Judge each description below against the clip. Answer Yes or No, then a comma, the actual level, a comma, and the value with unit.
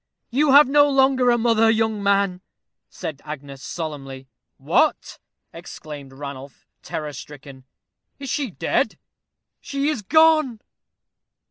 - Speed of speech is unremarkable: No, slow, 115 wpm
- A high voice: Yes, high, 205 Hz